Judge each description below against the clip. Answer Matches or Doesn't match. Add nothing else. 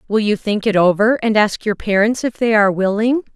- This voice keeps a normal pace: Doesn't match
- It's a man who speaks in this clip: Doesn't match